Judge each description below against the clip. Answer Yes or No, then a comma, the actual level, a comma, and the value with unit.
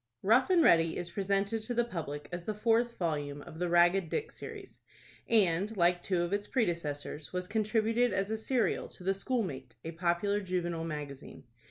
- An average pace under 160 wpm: No, average, 180 wpm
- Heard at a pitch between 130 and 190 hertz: Yes, medium, 185 Hz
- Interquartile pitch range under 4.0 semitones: No, average, 4.7 semitones